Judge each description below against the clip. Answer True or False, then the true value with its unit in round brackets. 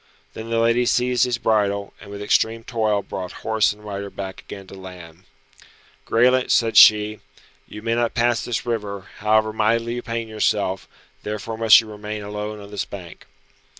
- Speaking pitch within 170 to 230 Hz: False (110 Hz)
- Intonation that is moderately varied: False (2.2 semitones)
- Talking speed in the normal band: True (175 wpm)